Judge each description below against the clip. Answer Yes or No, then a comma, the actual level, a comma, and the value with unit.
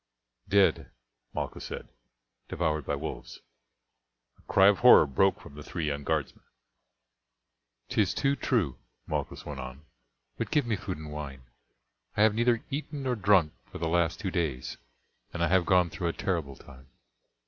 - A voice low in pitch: Yes, very low, 85 Hz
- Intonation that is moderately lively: No, wide, 5.7 semitones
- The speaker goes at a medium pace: Yes, average, 160 wpm